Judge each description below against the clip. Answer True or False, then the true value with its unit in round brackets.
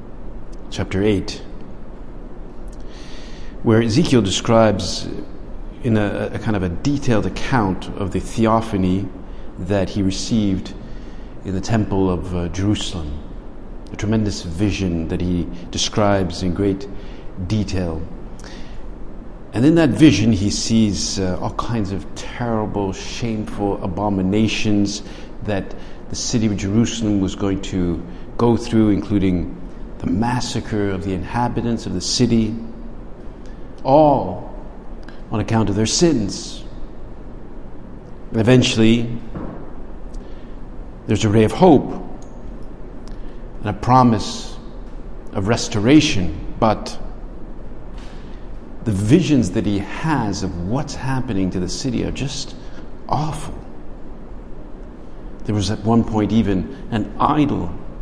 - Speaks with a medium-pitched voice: False (100 Hz)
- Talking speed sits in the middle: False (110 wpm)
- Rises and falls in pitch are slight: False (3.9 semitones)